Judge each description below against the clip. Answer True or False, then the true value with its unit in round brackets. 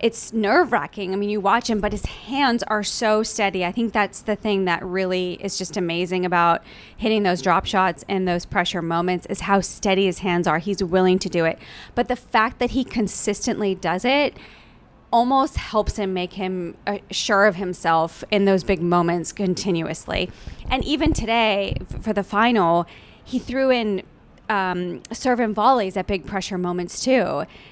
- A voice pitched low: False (200 Hz)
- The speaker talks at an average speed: True (180 wpm)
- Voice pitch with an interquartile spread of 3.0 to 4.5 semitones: True (3.5 semitones)